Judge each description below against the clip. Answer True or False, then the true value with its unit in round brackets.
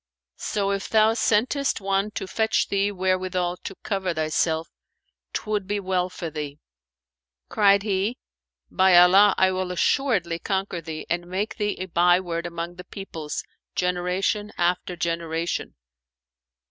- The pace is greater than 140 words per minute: False (135 wpm)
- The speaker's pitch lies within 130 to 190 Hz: True (185 Hz)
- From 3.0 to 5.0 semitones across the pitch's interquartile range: False (2.5 semitones)